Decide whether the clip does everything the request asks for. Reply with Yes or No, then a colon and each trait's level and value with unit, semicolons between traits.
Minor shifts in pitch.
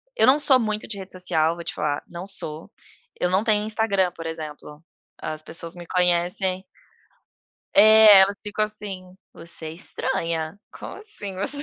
No: average, 4.0 semitones